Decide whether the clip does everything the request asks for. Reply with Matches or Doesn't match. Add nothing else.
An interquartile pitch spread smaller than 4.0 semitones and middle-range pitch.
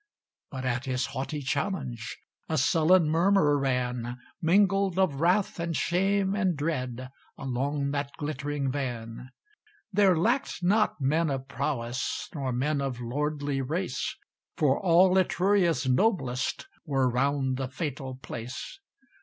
Doesn't match